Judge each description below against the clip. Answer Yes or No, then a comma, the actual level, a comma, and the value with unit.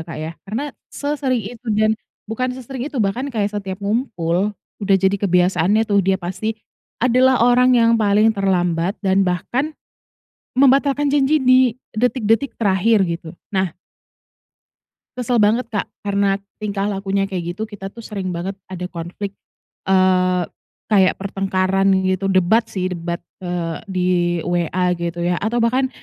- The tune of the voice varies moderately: Yes, average, 4.1 semitones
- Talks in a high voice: Yes, high, 200 Hz